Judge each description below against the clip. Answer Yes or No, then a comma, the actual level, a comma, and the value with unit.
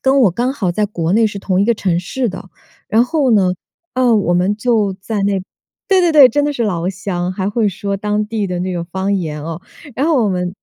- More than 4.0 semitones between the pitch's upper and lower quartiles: Yes, average, 4.4 semitones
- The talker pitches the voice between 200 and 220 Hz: Yes, high, 205 Hz